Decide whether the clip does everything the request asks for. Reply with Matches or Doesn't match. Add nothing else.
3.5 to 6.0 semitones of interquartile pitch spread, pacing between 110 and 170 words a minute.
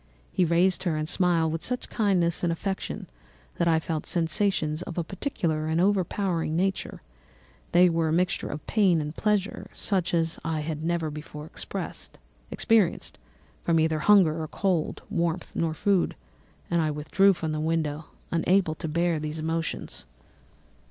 Doesn't match